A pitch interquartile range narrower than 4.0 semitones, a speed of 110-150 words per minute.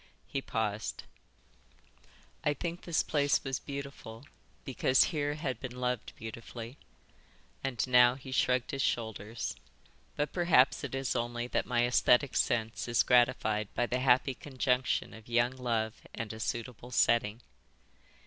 Yes: narrow, 2.4 semitones; average, 140 wpm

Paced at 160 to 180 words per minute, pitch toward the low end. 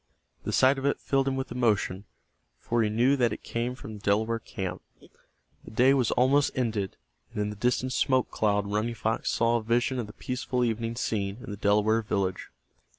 No: average, 200 wpm; low, 115 Hz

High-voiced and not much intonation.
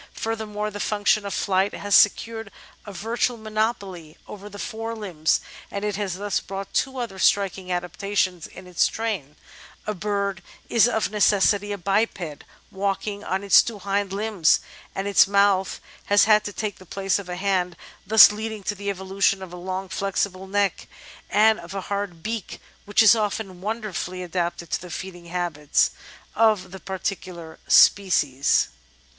Yes: high, 200 Hz; narrow, 2.3 semitones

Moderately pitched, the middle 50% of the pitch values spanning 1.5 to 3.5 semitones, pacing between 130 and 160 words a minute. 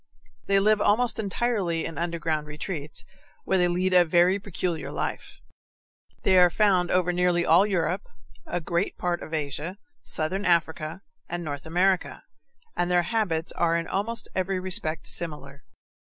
Yes: medium, 175 Hz; narrow, 2.6 semitones; average, 150 wpm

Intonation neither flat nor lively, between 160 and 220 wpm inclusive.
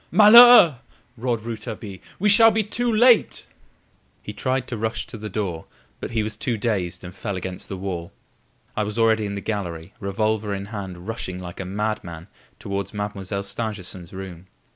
Yes: average, 3.5 semitones; average, 170 wpm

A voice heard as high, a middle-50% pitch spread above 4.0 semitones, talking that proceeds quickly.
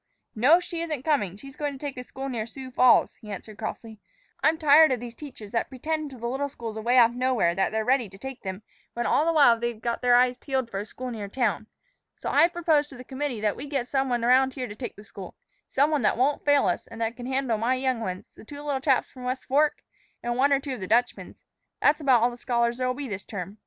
No: very high, 250 Hz; average, 3.4 semitones; fast, 265 wpm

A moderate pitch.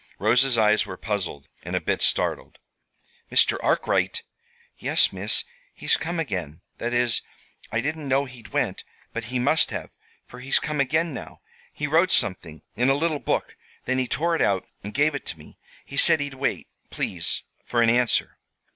No: low, 125 Hz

